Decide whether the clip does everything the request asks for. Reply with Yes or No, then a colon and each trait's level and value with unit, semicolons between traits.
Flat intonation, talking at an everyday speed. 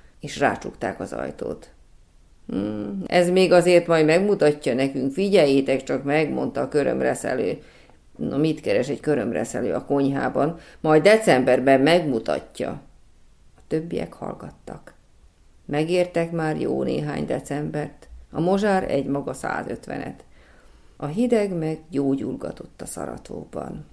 No: average, 4.5 semitones; average, 115 wpm